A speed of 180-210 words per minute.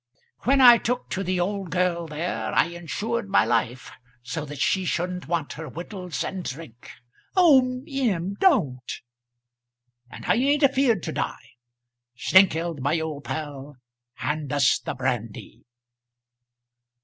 No: slow, 135 wpm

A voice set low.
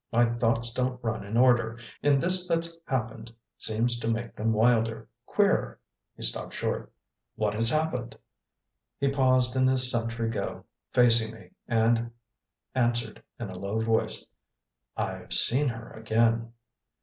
Yes: low, 115 Hz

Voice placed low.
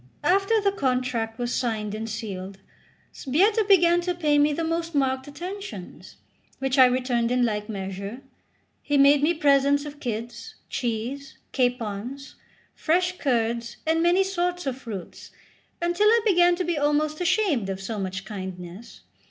No: very high, 275 Hz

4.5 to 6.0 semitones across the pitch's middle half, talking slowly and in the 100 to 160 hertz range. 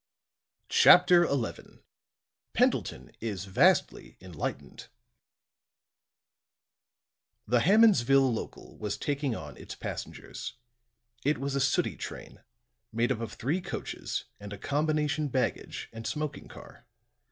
Yes: average, 5.1 semitones; slow, 105 wpm; low, 135 Hz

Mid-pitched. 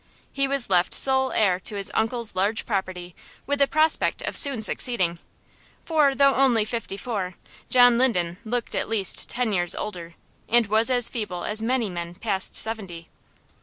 No: high, 220 Hz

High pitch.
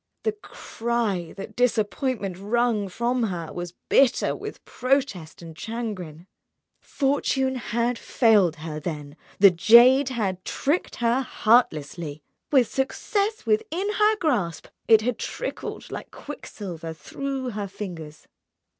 Yes: high, 225 Hz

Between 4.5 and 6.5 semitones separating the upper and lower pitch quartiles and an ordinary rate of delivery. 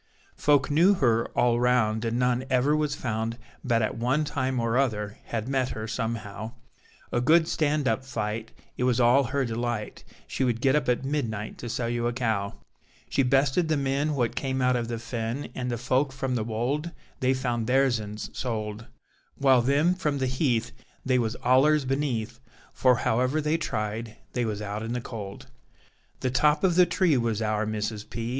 No: average, 3.2 semitones; average, 190 wpm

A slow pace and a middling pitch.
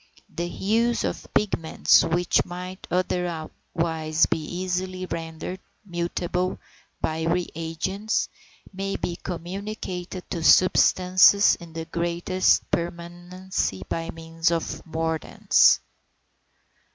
Yes: slow, 95 wpm; medium, 175 Hz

